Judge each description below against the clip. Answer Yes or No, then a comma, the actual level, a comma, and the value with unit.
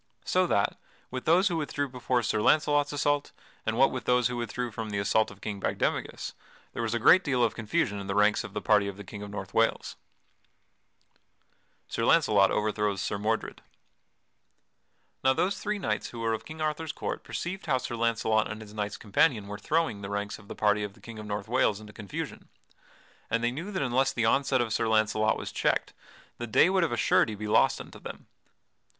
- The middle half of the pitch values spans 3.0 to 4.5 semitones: Yes, average, 4.2 semitones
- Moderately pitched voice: No, low, 115 Hz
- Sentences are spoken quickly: Yes, fast, 210 wpm